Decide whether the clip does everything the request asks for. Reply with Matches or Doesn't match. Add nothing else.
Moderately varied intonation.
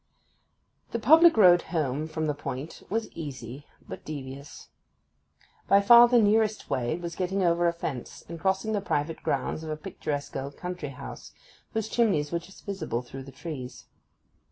Doesn't match